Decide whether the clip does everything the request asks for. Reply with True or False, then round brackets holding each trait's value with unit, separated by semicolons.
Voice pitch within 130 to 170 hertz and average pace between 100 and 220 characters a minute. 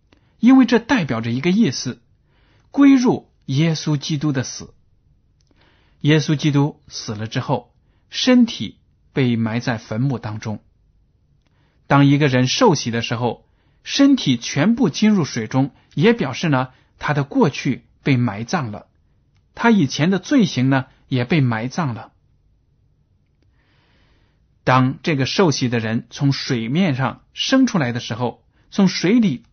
True (140 Hz; 195 characters per minute)